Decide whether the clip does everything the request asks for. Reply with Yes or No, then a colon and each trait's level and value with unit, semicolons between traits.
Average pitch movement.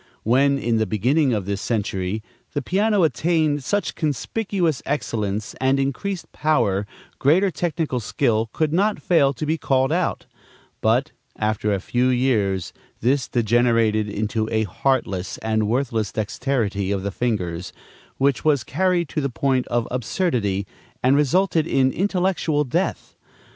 No: wide, 6.1 semitones